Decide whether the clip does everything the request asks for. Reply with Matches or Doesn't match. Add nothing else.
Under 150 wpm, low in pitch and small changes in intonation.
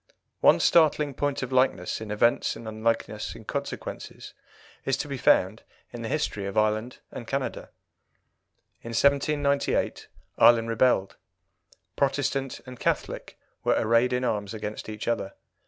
Doesn't match